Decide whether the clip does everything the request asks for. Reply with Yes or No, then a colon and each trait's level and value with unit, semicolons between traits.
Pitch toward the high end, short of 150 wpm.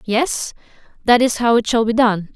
No: high, 230 Hz; fast, 205 wpm